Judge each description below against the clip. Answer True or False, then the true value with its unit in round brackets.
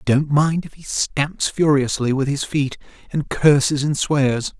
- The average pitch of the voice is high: False (140 Hz)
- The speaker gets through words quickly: False (170 wpm)